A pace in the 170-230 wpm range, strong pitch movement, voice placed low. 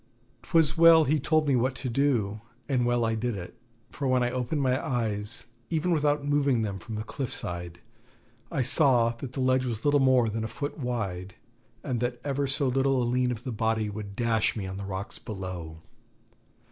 No: average, 200 wpm; average, 4.2 semitones; low, 125 Hz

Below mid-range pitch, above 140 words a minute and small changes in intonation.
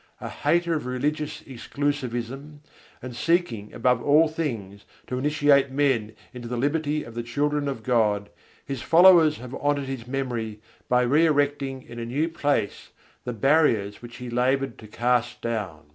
No: low, 130 Hz; average, 160 wpm; average, 3.7 semitones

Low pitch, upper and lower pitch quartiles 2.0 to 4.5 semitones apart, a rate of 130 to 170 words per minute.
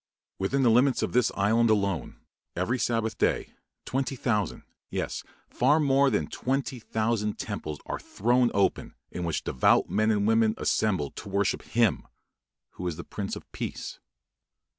Yes: low, 110 Hz; average, 3.9 semitones; average, 155 wpm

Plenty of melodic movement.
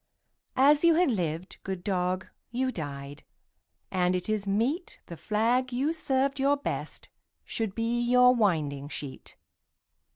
Yes: wide, 6.5 semitones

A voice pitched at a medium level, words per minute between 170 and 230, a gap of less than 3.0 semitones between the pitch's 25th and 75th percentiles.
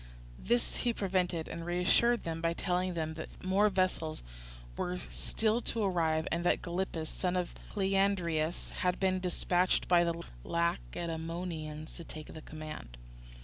No: medium, 175 Hz; average, 145 wpm; narrow, 2.5 semitones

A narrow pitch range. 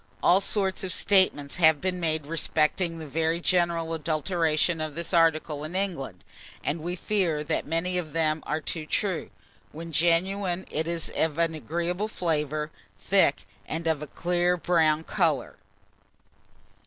Yes: narrow, 2.3 semitones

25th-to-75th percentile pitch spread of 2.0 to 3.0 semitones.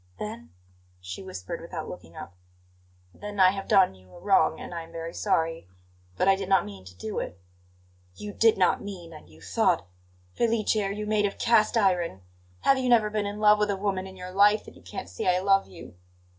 No: average, 4.2 semitones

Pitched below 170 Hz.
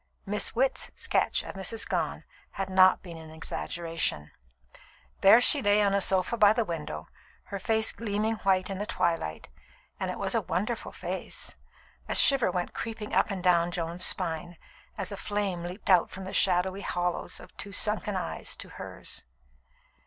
No: high, 190 Hz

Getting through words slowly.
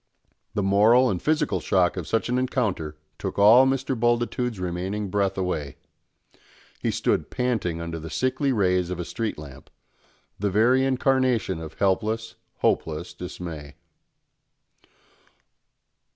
Yes: slow, 125 wpm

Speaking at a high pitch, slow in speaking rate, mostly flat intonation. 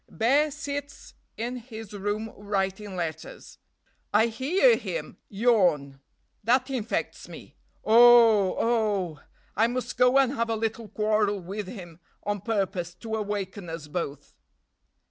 No: high, 215 Hz; slow, 125 wpm; average, 3.8 semitones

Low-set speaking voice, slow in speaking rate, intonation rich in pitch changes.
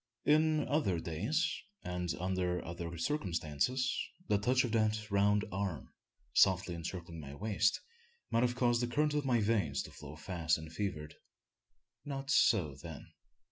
No: low, 100 Hz; average, 145 wpm; wide, 6.5 semitones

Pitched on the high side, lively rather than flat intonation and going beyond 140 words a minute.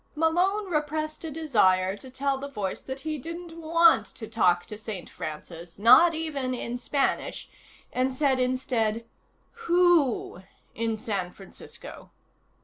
No: very high, 260 Hz; wide, 6.7 semitones; slow, 135 wpm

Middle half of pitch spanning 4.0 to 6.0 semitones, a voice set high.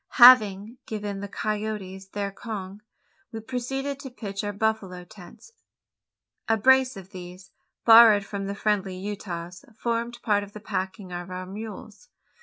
No: average, 2.7 semitones; high, 205 Hz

